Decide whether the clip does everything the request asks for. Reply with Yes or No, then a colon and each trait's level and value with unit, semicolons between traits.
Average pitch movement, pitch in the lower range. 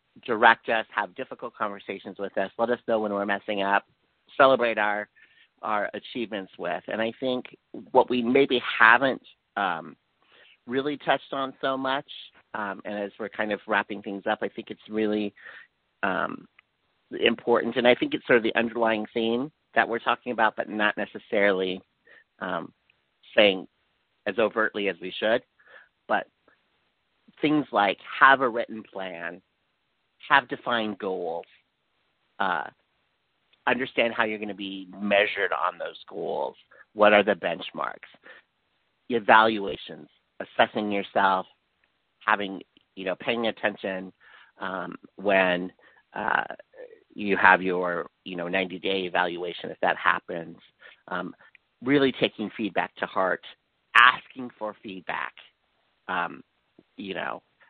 Yes: average, 3.4 semitones; low, 105 Hz